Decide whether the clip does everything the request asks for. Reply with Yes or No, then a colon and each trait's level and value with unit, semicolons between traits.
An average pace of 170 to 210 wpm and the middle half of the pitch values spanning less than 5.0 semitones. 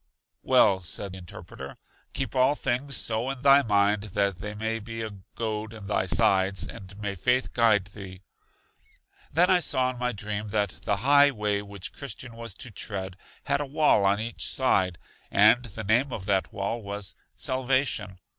Yes: average, 175 wpm; average, 3.9 semitones